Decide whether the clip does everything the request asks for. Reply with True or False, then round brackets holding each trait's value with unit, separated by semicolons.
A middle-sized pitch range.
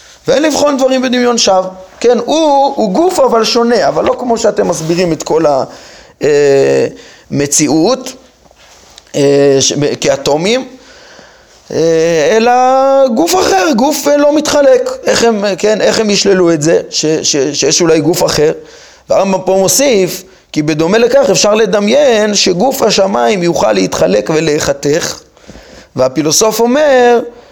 False (7.6 semitones)